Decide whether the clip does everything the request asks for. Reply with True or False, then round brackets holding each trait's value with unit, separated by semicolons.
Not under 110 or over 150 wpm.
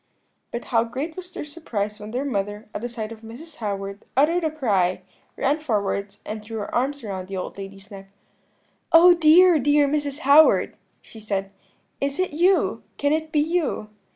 False (180 wpm)